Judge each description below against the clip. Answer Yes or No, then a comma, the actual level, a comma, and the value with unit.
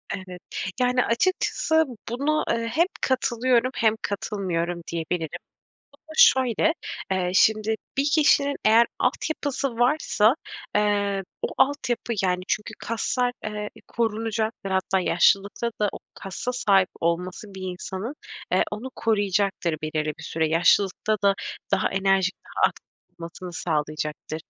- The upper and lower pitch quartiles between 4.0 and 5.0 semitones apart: Yes, average, 4.6 semitones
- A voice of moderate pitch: No, high, 210 Hz